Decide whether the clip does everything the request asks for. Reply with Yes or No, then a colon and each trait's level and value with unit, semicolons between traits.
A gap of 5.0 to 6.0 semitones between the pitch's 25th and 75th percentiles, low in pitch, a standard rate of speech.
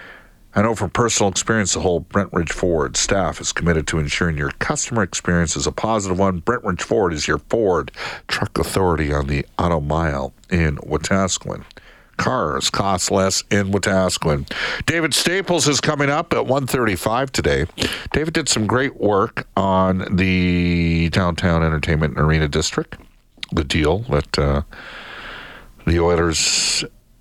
Yes: average, 5.3 semitones; very low, 95 Hz; average, 150 wpm